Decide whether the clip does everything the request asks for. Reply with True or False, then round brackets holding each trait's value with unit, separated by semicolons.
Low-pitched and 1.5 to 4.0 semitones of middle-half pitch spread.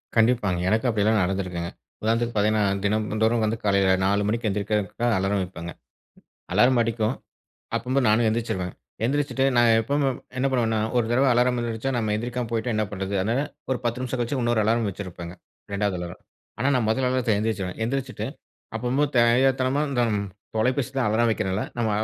True (115 Hz; 3.1 semitones)